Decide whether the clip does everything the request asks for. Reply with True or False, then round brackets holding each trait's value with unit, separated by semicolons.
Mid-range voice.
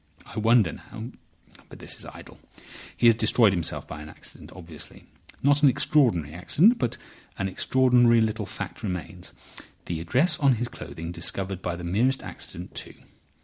False (110 Hz)